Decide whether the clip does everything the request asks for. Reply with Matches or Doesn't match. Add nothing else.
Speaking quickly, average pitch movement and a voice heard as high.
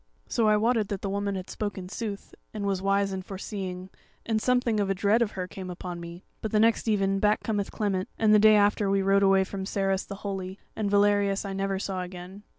Doesn't match